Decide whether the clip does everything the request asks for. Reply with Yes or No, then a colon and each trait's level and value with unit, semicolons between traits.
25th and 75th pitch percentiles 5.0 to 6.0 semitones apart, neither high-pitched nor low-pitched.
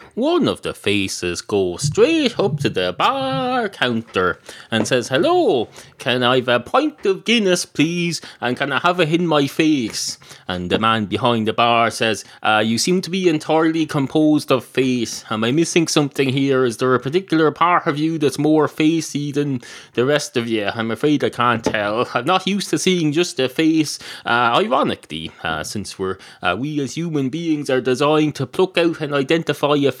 Yes: wide, 5.4 semitones; medium, 145 Hz